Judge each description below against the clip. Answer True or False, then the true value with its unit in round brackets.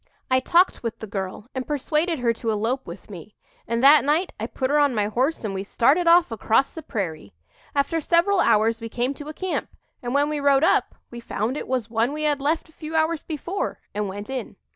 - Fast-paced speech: True (230 wpm)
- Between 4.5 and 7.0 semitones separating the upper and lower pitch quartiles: True (5.3 semitones)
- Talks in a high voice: True (265 Hz)